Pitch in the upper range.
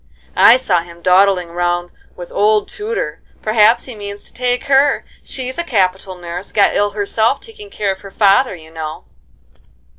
Yes: high, 200 Hz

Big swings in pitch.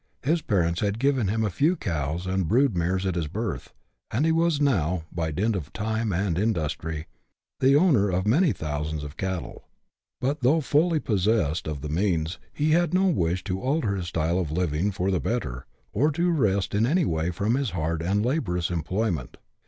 Yes: wide, 7.6 semitones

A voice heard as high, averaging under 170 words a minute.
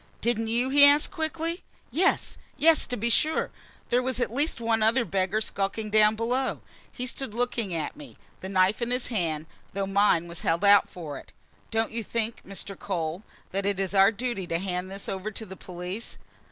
No: high, 215 Hz; average, 195 wpm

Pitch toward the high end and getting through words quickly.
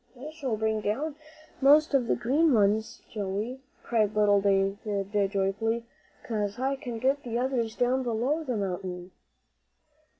No: high, 225 Hz; average, 140 wpm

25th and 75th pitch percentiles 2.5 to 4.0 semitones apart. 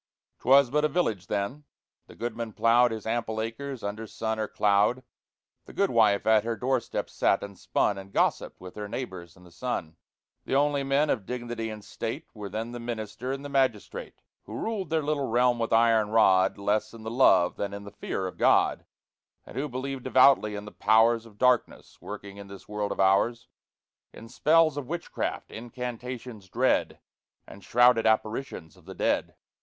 Yes: average, 3.7 semitones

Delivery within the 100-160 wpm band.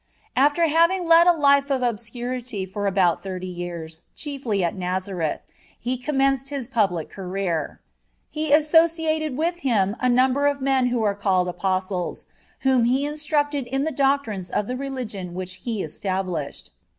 Yes: average, 150 wpm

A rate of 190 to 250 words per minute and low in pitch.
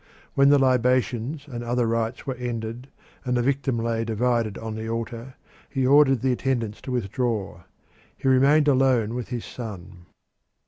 No: average, 155 wpm; low, 120 Hz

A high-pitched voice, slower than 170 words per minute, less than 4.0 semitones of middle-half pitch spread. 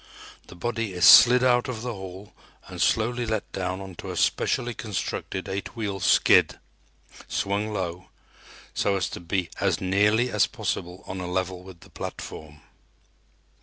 No: very low, 95 Hz; average, 155 wpm; average, 3.3 semitones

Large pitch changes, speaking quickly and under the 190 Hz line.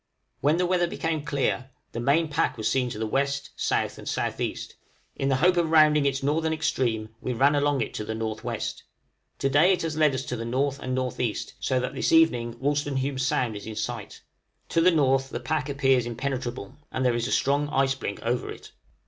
No: average, 3.6 semitones; fast, 210 wpm; low, 135 Hz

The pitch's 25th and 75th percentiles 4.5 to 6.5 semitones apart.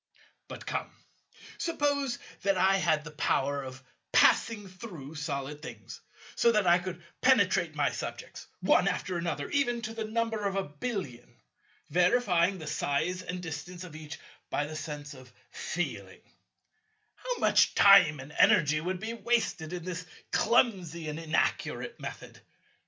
Yes: wide, 5.5 semitones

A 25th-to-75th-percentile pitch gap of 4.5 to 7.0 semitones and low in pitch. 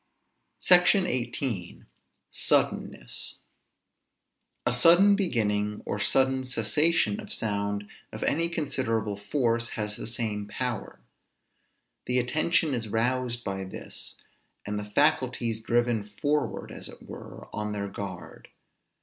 Yes: average, 5.3 semitones; low, 120 Hz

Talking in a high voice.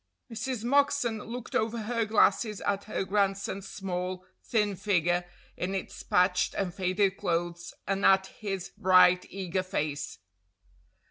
Yes: high, 195 Hz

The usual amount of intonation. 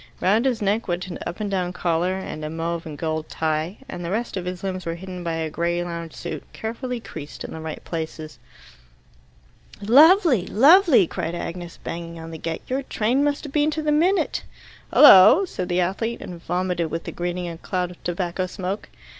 Yes: average, 4.9 semitones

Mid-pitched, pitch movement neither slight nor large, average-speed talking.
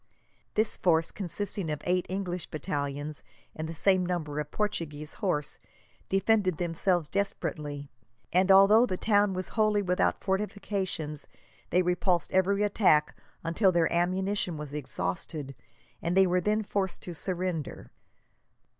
No: medium, 180 Hz; average, 4.0 semitones; slow, 130 wpm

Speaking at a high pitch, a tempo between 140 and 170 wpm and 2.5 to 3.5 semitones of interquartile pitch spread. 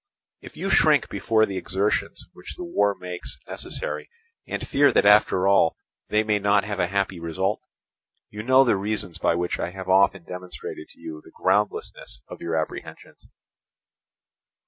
No: very low, 95 Hz; average, 165 wpm; average, 2.9 semitones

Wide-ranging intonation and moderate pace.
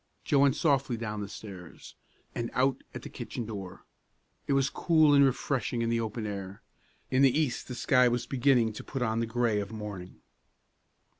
No: average, 4.0 semitones; average, 190 wpm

